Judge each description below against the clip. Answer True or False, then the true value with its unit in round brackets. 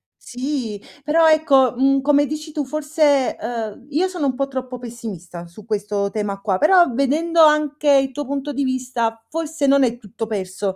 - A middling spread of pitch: True (4.8 semitones)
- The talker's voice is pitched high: True (265 Hz)